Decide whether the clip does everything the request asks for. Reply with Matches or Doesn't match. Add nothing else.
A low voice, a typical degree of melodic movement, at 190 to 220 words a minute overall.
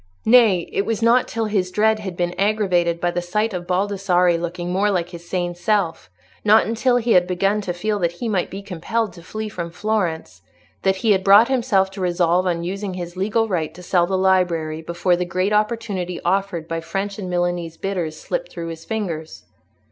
Doesn't match